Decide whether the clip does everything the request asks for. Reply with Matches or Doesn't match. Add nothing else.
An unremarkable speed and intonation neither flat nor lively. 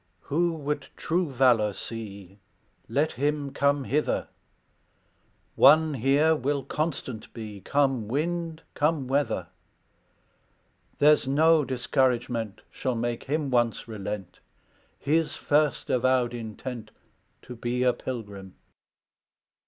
Doesn't match